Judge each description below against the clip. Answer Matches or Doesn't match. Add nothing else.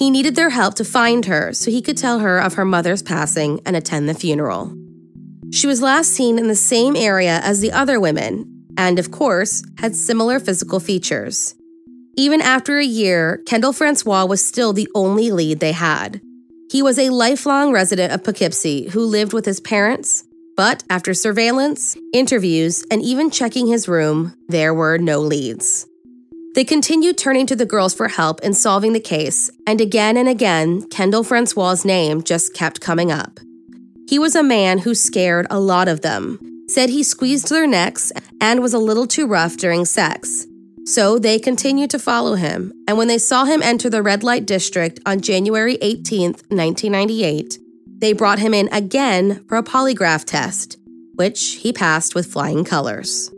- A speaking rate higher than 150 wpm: Matches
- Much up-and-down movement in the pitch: Matches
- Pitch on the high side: Matches